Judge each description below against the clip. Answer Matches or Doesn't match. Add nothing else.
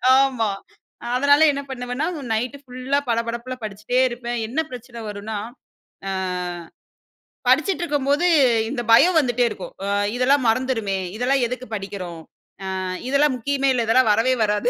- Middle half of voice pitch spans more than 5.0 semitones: Doesn't match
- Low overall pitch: Doesn't match